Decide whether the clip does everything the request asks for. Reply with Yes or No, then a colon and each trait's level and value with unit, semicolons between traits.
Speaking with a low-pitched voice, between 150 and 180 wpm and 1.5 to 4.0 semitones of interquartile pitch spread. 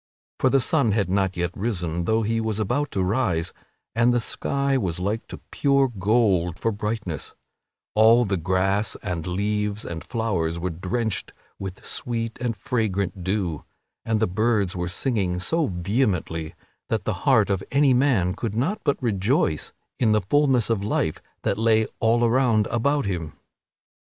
No: low, 105 Hz; average, 160 wpm; average, 4.4 semitones